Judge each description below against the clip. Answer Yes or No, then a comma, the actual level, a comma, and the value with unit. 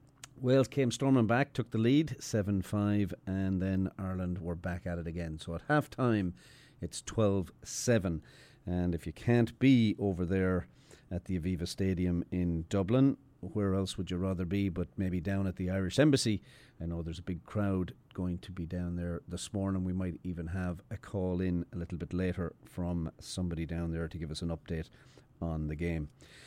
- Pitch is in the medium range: No, very low, 95 Hz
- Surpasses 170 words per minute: Yes, average, 195 wpm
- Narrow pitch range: No, average, 3.7 semitones